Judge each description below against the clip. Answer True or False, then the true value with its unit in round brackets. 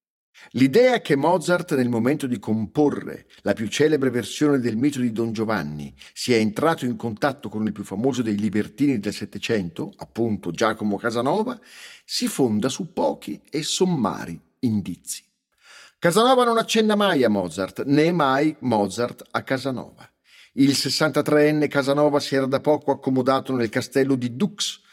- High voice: False (135 Hz)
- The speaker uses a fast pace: False (145 wpm)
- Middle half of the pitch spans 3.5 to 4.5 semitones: False (5.3 semitones)